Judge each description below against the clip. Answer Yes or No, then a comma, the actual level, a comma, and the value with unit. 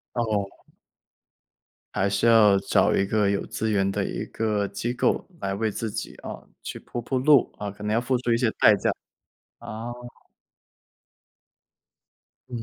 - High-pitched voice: No, low, 110 Hz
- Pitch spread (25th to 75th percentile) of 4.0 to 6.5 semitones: No, average, 2.8 semitones